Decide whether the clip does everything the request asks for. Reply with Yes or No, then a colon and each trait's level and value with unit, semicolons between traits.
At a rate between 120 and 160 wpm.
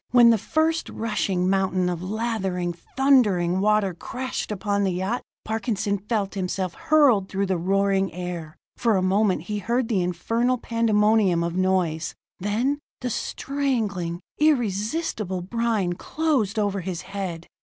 Yes: slow, 135 wpm